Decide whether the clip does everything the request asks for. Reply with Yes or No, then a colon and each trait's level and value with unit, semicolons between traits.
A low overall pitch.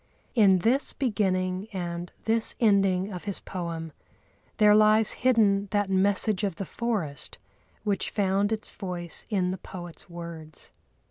No: high, 195 Hz